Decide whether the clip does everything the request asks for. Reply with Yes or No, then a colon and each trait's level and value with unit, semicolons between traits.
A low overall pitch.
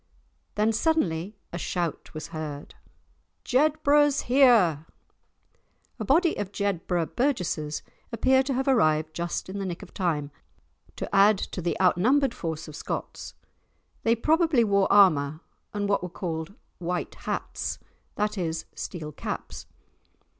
No: high, 195 Hz